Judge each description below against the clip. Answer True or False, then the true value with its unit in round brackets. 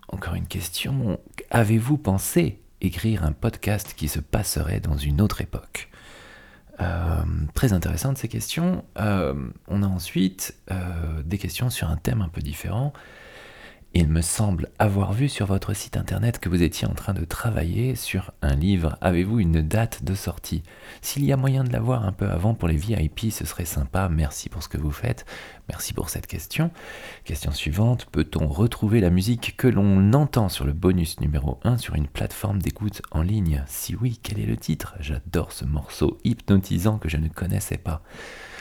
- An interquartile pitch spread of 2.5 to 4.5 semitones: False (5.2 semitones)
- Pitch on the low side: True (95 Hz)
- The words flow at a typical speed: True (180 wpm)